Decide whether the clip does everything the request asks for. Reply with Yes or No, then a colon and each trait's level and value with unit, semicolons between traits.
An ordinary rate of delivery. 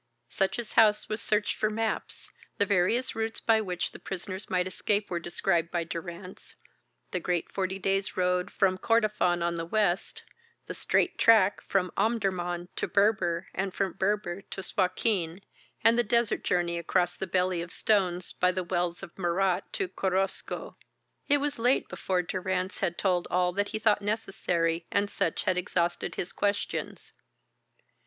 Yes: average, 160 wpm